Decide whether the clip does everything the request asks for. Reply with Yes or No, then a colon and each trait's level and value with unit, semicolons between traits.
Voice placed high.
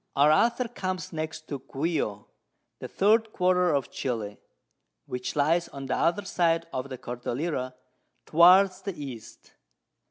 No: medium, 160 Hz